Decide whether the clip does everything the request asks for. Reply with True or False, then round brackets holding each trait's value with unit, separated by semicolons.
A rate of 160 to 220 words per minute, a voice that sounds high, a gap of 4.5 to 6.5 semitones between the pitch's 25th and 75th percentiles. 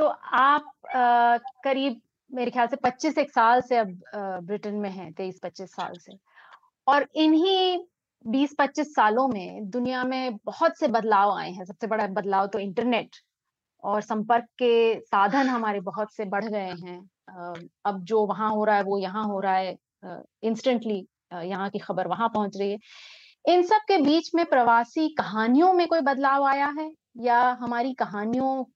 True (165 wpm; 235 Hz; 5.1 semitones)